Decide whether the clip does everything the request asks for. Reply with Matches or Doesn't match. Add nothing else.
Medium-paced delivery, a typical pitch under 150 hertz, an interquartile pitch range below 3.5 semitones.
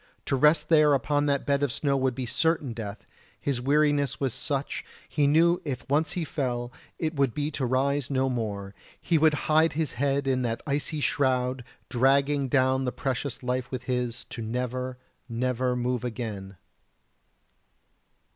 Matches